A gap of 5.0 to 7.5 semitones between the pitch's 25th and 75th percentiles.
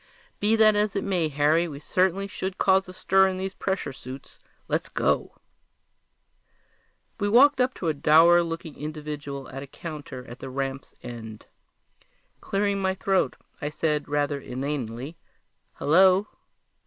Yes: average, 5.3 semitones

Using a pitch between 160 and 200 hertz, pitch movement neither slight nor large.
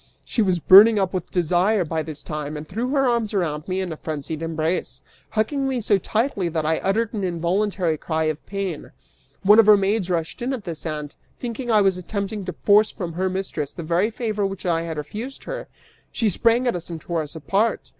Yes: high, 190 Hz; average, 4.8 semitones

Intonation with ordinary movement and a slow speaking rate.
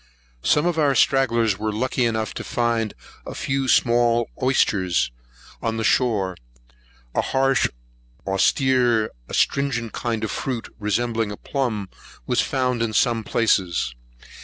Yes: average, 3.1 semitones; slow, 130 wpm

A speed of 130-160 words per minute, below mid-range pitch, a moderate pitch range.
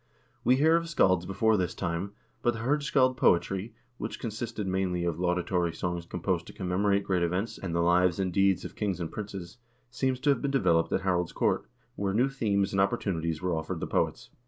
No: average, 200 wpm; very low, 95 Hz; average, 4.1 semitones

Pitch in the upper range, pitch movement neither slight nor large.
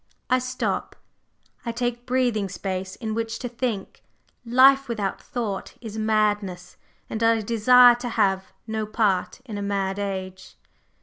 Yes: high, 220 Hz; average, 3.5 semitones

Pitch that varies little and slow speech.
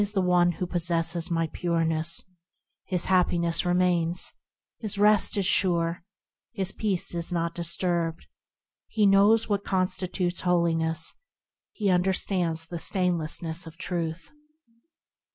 Yes: narrow, 2.0 semitones; slow, 115 wpm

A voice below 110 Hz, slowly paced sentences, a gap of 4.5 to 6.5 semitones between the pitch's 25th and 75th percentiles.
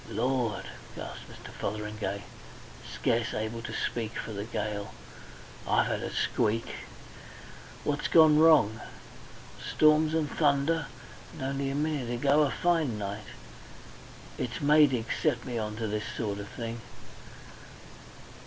No: low, 120 Hz; slow, 125 wpm; wide, 5.5 semitones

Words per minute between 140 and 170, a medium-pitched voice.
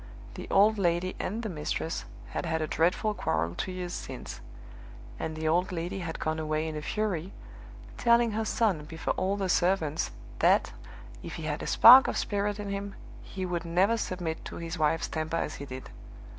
No: average, 190 wpm; medium, 175 Hz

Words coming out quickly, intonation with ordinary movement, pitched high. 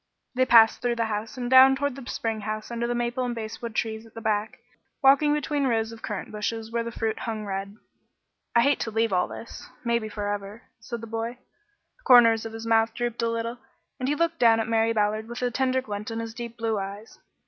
No: fast, 225 wpm; narrow, 1.7 semitones; high, 230 Hz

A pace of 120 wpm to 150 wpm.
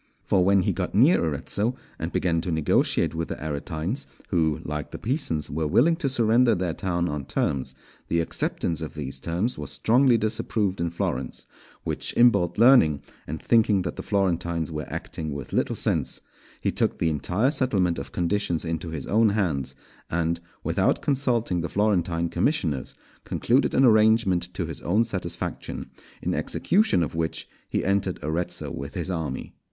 No: average, 165 wpm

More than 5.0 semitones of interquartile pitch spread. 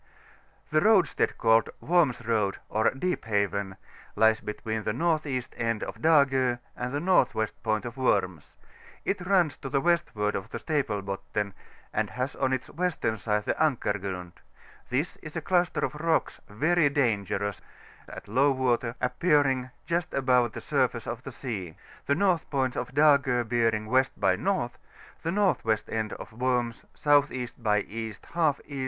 Yes: wide, 5.5 semitones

